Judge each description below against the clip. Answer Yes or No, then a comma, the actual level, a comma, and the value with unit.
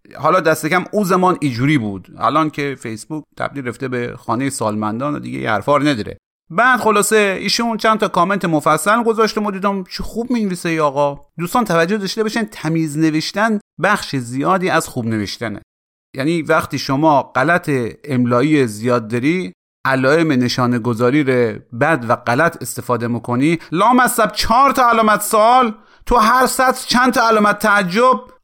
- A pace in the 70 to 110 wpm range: No, fast, 155 wpm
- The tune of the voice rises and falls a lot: Yes, wide, 8.4 semitones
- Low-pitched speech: No, medium, 160 Hz